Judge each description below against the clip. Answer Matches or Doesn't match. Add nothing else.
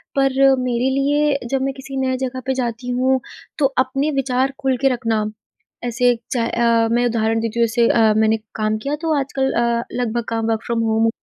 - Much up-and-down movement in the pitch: Doesn't match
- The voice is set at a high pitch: Matches